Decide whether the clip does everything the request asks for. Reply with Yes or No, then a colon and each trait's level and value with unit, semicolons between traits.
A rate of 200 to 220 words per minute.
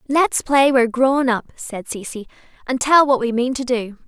Yes: fast, 205 wpm